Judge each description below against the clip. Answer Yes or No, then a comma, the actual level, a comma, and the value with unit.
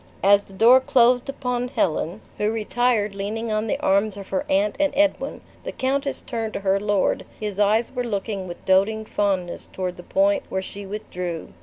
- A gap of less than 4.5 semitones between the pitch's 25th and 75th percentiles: Yes, average, 3.4 semitones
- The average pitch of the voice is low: No, high, 210 Hz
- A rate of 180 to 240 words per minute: Yes, average, 185 wpm